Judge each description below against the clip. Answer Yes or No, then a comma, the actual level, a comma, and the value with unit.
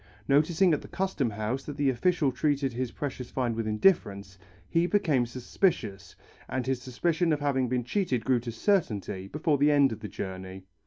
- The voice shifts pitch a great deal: No, average, 4.9 semitones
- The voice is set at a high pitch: No, low, 130 Hz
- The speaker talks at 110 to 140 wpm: No, average, 180 wpm